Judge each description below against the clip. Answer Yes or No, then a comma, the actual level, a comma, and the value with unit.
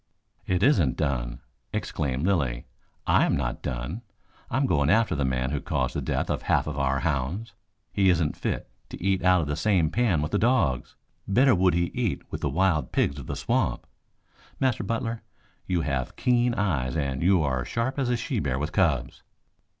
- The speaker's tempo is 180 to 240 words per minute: Yes, average, 195 wpm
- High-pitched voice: No, very low, 85 Hz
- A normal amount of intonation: No, wide, 7.1 semitones